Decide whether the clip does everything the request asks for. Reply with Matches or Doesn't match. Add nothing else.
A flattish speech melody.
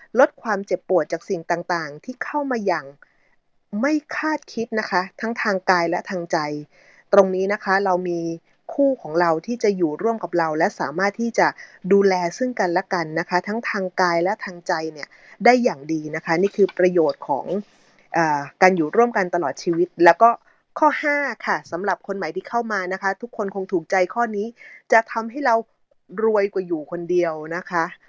Doesn't match